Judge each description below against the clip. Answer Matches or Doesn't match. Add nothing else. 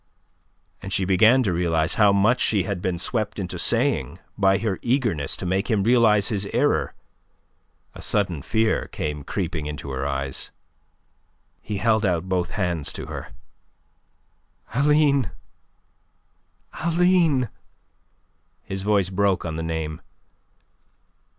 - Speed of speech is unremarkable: Doesn't match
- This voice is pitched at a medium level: Doesn't match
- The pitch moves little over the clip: Doesn't match